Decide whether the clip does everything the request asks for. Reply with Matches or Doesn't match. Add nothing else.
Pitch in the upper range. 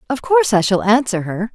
Matches